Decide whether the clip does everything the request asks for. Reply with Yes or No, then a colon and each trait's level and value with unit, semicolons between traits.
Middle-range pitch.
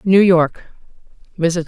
Yes: medium, 175 Hz